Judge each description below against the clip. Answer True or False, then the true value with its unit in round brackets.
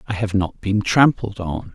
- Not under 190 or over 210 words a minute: True (205 wpm)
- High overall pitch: False (105 Hz)